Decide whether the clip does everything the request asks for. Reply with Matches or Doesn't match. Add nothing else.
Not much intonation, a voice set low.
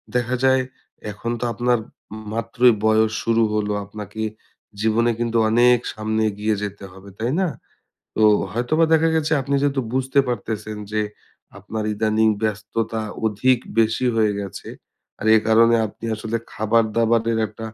Matches